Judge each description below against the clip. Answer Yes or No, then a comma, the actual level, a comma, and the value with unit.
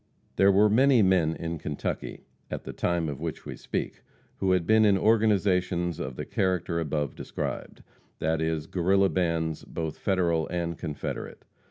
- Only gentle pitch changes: No, average, 3.2 semitones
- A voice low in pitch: Yes, very low, 85 Hz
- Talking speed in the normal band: Yes, average, 160 wpm